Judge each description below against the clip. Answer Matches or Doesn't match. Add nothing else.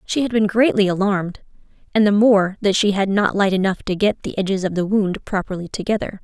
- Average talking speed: Doesn't match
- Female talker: Matches